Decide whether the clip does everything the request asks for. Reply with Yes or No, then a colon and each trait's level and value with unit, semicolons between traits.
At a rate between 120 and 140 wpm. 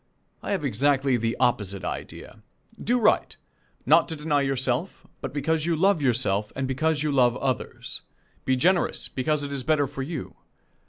No: average, 165 wpm